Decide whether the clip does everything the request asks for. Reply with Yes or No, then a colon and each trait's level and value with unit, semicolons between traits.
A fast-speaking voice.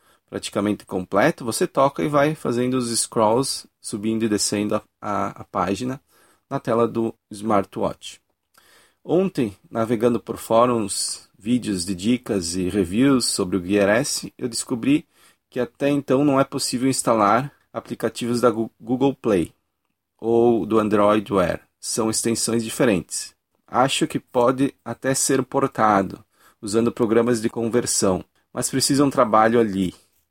No: average, 135 wpm